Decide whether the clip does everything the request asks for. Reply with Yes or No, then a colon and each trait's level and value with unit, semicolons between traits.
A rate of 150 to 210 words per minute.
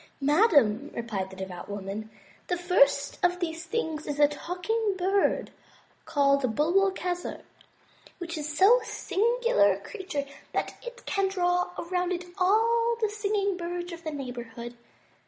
Yes: average, 155 wpm